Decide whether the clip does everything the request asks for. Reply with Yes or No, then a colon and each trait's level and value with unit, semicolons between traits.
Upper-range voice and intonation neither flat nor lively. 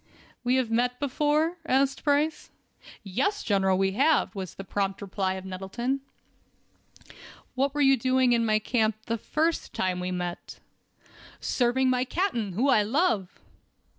No: high, 245 Hz; wide, 5.8 semitones